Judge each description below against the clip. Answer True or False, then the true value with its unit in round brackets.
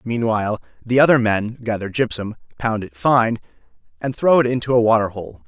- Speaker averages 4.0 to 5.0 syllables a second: False (5.4 syllables/s)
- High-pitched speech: False (115 Hz)